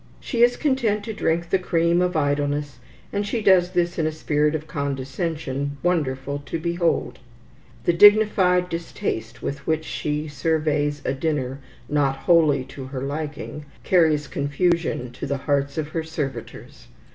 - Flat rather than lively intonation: No, average, 3.5 semitones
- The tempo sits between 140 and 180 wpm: Yes, average, 150 wpm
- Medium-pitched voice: Yes, medium, 155 Hz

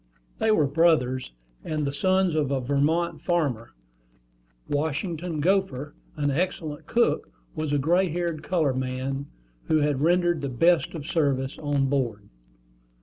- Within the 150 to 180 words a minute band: No, average, 140 wpm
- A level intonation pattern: No, average, 3.8 semitones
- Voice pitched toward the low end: No, medium, 150 Hz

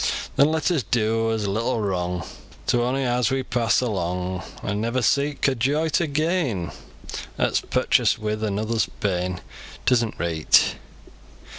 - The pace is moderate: Yes, average, 145 wpm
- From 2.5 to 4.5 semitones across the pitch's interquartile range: No, average, 5.1 semitones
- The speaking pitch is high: No, low, 115 Hz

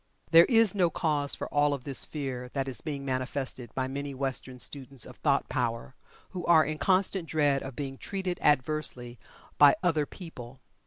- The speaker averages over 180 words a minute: No, average, 175 wpm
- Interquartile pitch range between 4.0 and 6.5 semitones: No, average, 3.3 semitones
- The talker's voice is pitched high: No, medium, 140 Hz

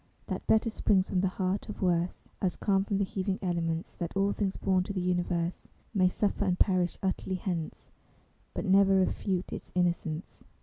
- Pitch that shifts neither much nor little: No, narrow, 1.7 semitones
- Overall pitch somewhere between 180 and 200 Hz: Yes, medium, 185 Hz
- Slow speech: No, average, 180 wpm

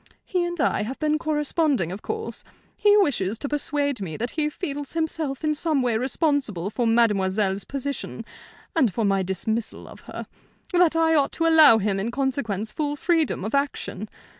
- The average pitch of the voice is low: No, very high, 275 Hz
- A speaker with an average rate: Yes, average, 175 wpm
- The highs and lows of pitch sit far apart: Yes, wide, 6.3 semitones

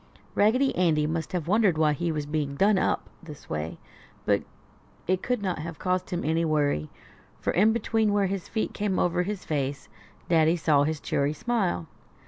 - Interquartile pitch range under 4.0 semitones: No, average, 4.7 semitones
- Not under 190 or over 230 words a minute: No, average, 180 wpm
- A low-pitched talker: No, medium, 170 Hz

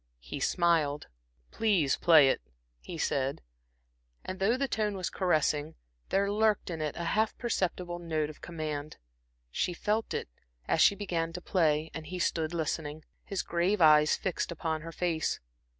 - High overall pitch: No, medium, 170 Hz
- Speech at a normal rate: Yes, average, 160 wpm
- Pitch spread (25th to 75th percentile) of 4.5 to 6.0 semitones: No, average, 3.4 semitones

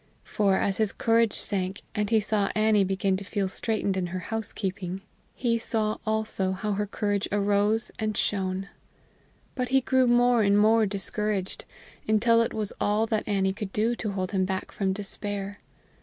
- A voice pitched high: Yes, high, 205 Hz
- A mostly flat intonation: Yes, narrow, 2.1 semitones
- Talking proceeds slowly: No, average, 170 wpm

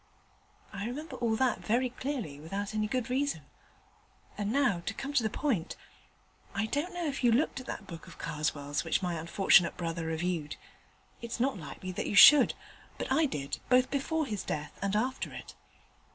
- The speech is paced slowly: No, average, 180 wpm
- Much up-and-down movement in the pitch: Yes, wide, 7.4 semitones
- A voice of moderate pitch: No, high, 215 Hz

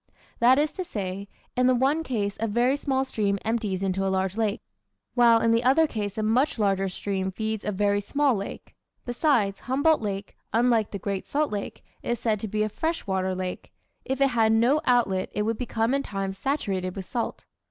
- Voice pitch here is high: Yes, high, 220 Hz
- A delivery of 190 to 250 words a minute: Yes, fast, 205 wpm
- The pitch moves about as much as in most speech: Yes, average, 4.3 semitones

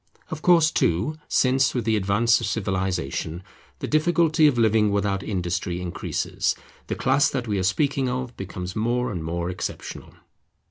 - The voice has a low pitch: Yes, low, 110 Hz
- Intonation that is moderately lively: No, wide, 6.1 semitones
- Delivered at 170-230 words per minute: No, average, 155 wpm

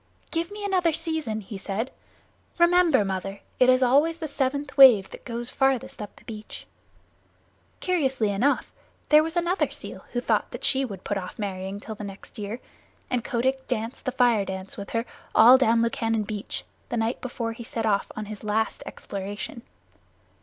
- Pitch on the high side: Yes, high, 235 Hz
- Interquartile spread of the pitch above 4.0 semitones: Yes, average, 4.5 semitones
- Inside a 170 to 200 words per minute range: Yes, average, 175 wpm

